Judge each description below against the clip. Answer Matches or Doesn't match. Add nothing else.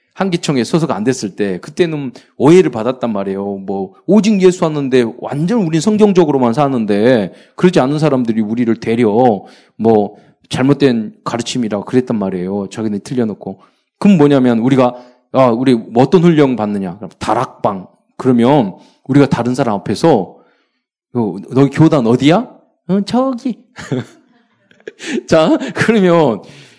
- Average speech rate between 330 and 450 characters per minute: Doesn't match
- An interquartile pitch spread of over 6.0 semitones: Matches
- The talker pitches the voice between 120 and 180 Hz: Matches